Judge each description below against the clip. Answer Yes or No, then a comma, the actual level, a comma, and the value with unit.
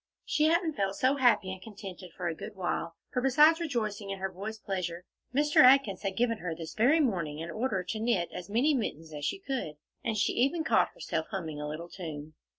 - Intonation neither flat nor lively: No, wide, 6.7 semitones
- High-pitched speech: Yes, high, 200 Hz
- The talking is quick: Yes, fast, 215 wpm